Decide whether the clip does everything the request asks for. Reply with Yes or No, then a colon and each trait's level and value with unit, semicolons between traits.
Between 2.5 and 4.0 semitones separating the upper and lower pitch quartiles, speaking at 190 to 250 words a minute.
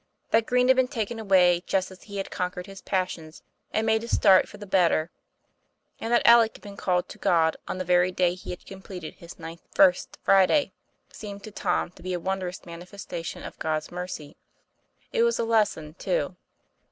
Yes: average, 3.6 semitones; average, 195 wpm